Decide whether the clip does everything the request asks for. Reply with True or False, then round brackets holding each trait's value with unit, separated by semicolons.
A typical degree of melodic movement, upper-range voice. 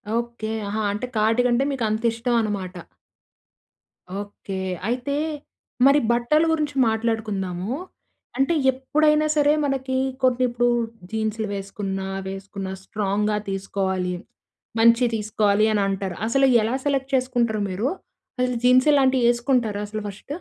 True (4.1 semitones; 225 Hz)